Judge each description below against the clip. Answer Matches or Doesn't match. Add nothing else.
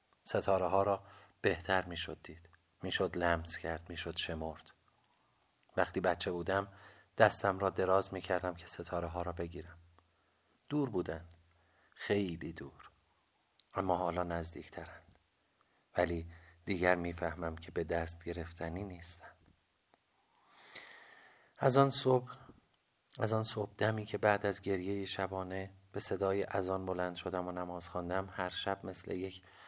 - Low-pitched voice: Matches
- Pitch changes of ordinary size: Doesn't match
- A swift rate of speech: Doesn't match